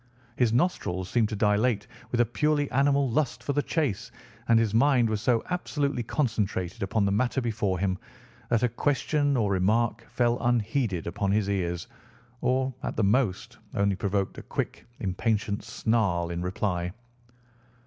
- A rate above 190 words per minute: No, average, 160 wpm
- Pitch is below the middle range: Yes, low, 110 Hz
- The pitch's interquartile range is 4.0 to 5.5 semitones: Yes, average, 4.3 semitones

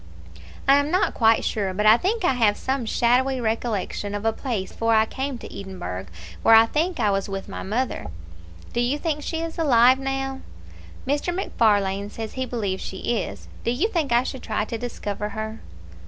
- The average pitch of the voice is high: Yes, high, 235 Hz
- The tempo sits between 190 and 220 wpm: Yes, average, 195 wpm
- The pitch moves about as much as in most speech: Yes, average, 4.4 semitones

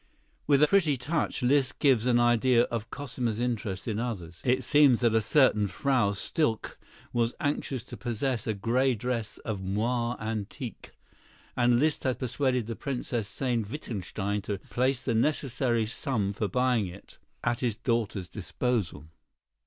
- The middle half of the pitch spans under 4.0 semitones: Yes, average, 3.2 semitones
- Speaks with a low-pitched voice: Yes, low, 120 Hz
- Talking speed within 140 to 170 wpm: Yes, average, 155 wpm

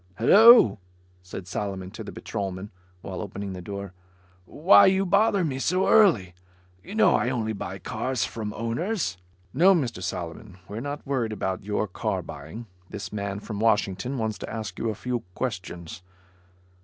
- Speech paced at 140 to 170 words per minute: Yes, average, 160 wpm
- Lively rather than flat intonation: Yes, wide, 5.7 semitones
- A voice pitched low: Yes, low, 110 Hz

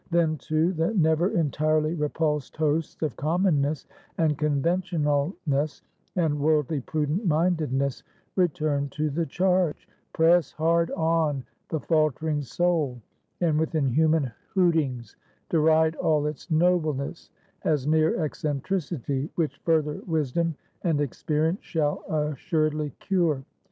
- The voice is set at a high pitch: No, medium, 155 Hz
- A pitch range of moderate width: No, narrow, 2.1 semitones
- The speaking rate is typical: No, slow, 110 wpm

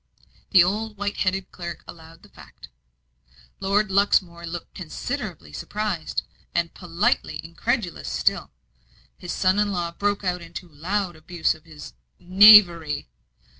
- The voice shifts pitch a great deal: No, average, 3.3 semitones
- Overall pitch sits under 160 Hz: No, medium, 180 Hz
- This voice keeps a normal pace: No, slow, 130 wpm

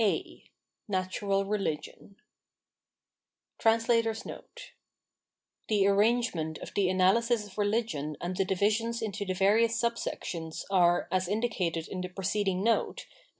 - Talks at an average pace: No, slow, 110 wpm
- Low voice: No, high, 200 Hz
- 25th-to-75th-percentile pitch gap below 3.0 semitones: No, average, 3.5 semitones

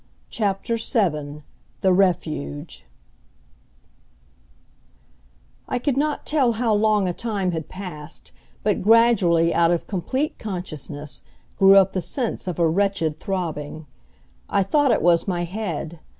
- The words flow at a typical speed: No, slow, 125 wpm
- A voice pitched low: No, medium, 185 Hz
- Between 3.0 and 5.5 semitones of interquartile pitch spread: Yes, average, 4.7 semitones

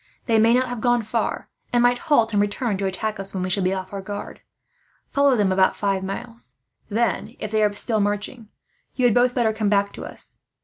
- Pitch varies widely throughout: No, average, 3.2 semitones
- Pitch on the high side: Yes, high, 215 Hz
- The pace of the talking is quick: Yes, fast, 225 wpm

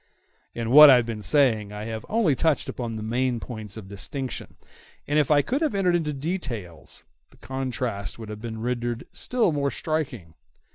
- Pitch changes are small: No, average, 5.2 semitones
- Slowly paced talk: No, average, 185 wpm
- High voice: No, low, 125 Hz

